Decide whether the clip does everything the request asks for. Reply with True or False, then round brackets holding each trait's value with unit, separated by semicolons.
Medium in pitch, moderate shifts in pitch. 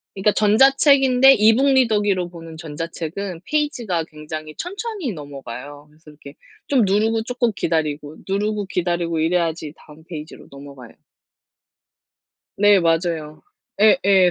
False (180 Hz; 6.0 semitones)